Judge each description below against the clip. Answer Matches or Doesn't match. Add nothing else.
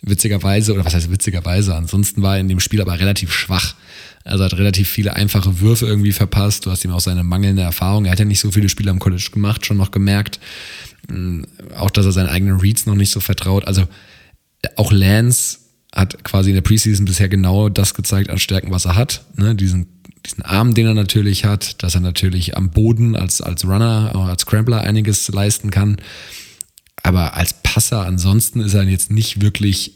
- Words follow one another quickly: Matches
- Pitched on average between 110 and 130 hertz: Doesn't match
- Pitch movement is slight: Matches